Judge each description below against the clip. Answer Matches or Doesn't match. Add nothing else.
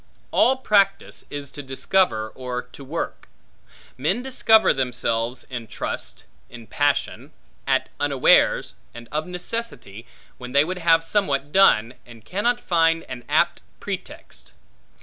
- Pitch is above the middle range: Doesn't match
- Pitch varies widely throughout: Matches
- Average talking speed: Doesn't match